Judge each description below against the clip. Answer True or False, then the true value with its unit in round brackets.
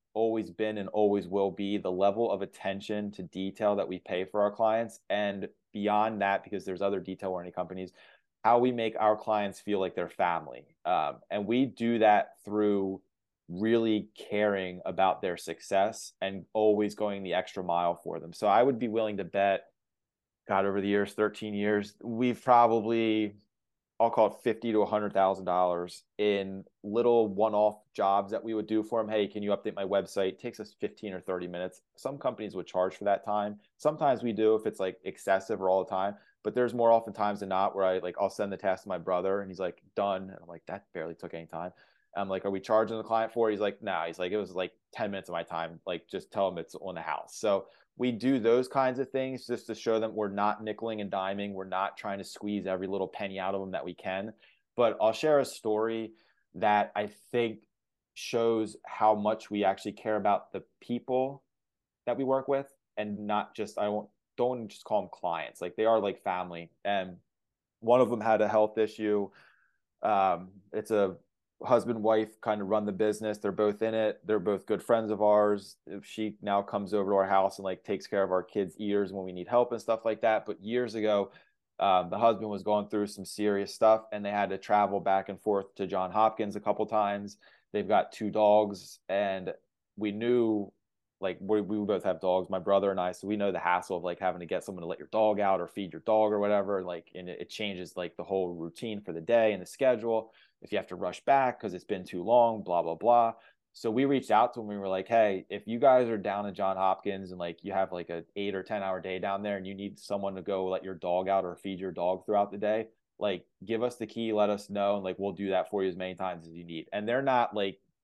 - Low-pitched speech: True (105 Hz)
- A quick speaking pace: True (235 wpm)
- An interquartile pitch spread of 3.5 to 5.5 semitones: False (2.4 semitones)